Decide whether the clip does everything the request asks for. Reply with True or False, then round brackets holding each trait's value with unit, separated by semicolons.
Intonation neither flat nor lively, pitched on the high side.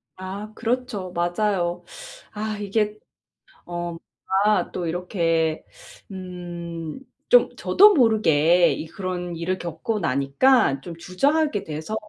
False (3.9 semitones; 180 Hz)